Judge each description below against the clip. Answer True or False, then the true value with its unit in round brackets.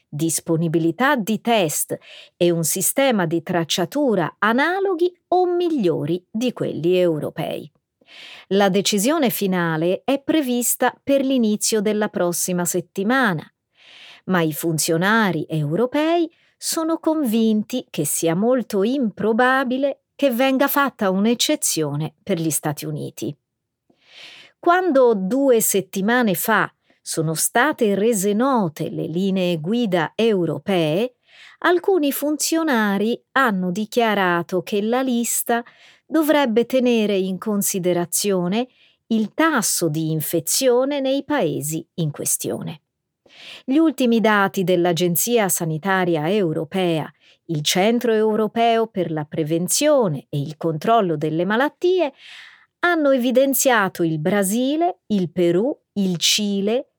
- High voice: True (210 Hz)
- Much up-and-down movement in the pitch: True (6.7 semitones)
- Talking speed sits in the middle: False (105 wpm)